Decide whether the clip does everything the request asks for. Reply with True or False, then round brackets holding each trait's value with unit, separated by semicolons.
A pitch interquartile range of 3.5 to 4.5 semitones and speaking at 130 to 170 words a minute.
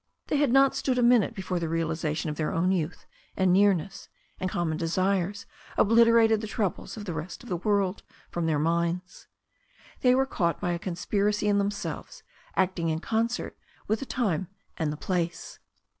False (4.1 semitones; 180 wpm)